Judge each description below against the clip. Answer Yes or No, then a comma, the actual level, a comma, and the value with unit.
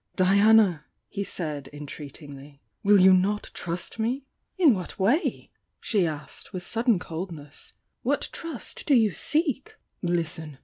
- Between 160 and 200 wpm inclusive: No, average, 140 wpm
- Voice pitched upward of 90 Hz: Yes, medium, 185 Hz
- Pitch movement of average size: No, wide, 5.8 semitones